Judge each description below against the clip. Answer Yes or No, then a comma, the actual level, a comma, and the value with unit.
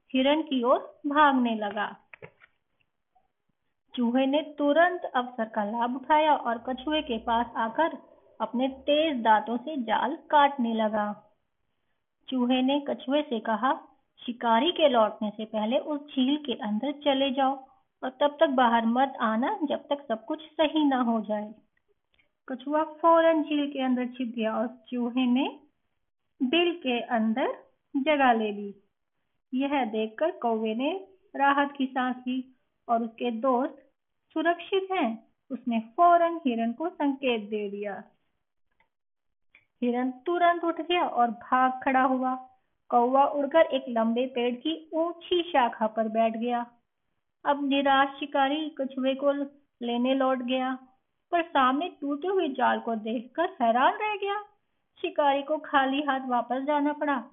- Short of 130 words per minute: No, average, 140 wpm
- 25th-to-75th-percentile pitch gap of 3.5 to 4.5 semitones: Yes, average, 4.1 semitones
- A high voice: Yes, very high, 265 Hz